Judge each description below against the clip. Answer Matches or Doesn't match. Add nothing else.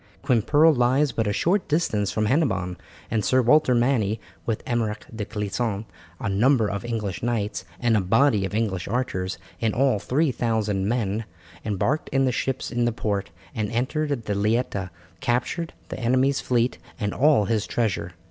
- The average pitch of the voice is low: Matches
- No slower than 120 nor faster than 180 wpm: Matches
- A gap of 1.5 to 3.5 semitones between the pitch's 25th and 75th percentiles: Doesn't match